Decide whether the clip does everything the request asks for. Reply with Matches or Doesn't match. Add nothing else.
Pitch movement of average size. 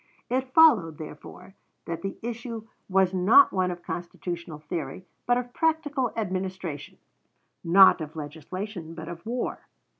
Doesn't match